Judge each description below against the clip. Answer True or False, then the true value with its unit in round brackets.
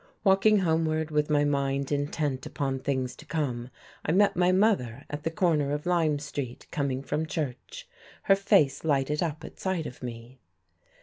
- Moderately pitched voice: True (150 Hz)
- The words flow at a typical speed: True (170 wpm)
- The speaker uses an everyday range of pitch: True (3.6 semitones)